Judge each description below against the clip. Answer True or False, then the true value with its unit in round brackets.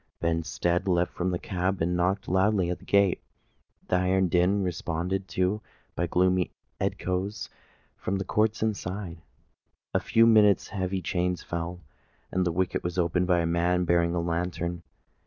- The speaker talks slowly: False (165 wpm)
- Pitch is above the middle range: False (90 Hz)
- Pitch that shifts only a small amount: True (1.6 semitones)